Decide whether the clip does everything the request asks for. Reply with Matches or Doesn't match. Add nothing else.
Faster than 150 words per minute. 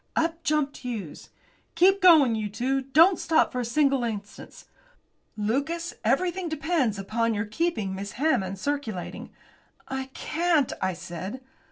Doesn't match